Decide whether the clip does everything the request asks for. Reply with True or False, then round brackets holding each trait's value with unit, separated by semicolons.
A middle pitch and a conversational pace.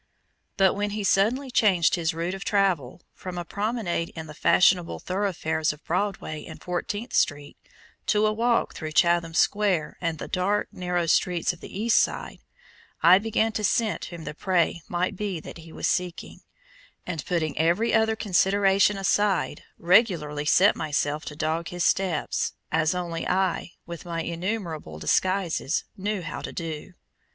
True (180 Hz; 160 wpm)